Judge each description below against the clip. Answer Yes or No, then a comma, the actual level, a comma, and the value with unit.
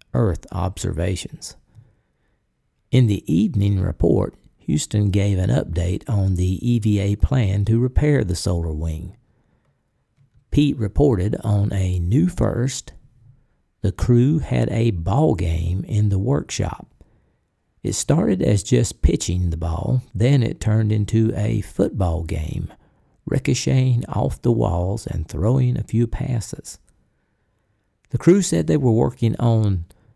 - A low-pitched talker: Yes, low, 110 Hz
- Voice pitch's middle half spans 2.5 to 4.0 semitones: No, average, 4.6 semitones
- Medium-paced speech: No, slow, 125 wpm